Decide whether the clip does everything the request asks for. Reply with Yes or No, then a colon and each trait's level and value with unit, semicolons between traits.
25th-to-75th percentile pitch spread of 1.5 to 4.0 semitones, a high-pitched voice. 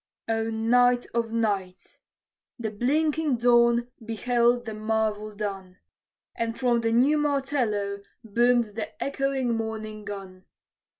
Yes: narrow, 2.5 semitones; high, 230 Hz